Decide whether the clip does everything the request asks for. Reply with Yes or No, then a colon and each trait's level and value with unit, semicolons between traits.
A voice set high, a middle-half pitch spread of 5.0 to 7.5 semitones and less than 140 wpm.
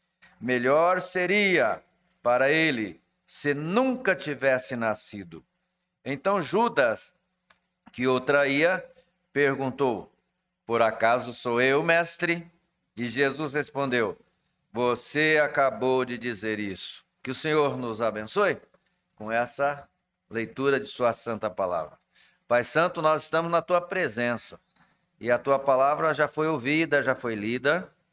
No: medium, 140 Hz; wide, 5.6 semitones; slow, 120 wpm